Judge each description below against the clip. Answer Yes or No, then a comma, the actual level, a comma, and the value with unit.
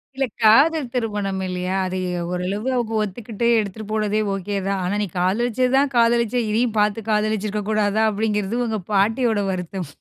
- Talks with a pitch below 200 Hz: No, high, 215 Hz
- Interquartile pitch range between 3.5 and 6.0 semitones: No, average, 2.7 semitones